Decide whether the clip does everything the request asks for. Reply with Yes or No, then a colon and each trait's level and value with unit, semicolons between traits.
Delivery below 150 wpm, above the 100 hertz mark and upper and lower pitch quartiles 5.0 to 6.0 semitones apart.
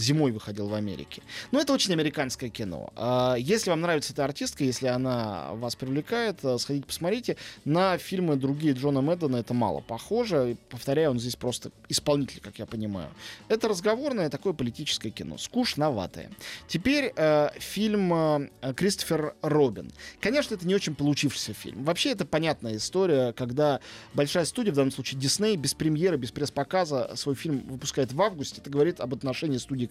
No: fast, 160 wpm; medium, 140 Hz; wide, 5.6 semitones